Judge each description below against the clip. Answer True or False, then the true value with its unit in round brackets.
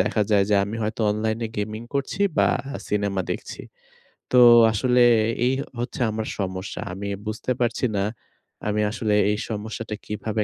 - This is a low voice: True (110 Hz)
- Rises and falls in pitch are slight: True (1.6 semitones)